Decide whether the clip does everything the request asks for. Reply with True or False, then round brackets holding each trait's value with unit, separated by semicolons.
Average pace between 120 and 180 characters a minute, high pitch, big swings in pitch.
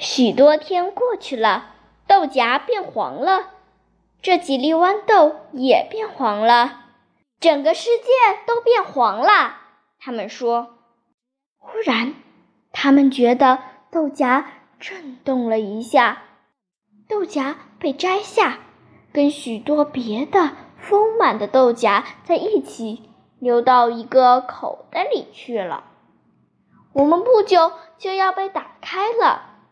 True (165 characters per minute; 290 Hz; 7.6 semitones)